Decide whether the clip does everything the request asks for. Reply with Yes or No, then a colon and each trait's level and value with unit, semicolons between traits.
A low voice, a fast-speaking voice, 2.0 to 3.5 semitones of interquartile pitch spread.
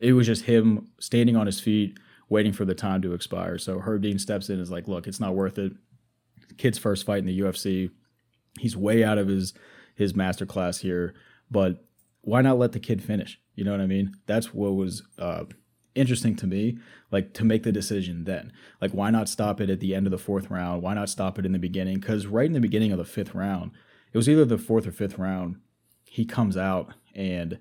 Yes: low, 100 Hz; fast, 235 wpm; average, 2.9 semitones